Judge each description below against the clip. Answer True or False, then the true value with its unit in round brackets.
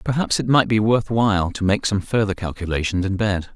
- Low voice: True (105 Hz)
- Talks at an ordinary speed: False (220 wpm)